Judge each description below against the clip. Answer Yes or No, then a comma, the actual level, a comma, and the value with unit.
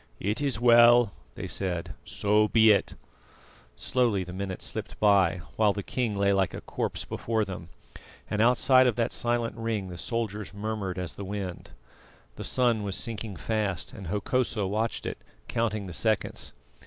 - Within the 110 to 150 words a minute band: No, average, 165 wpm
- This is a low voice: Yes, low, 105 Hz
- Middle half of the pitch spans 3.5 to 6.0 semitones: No, average, 3.0 semitones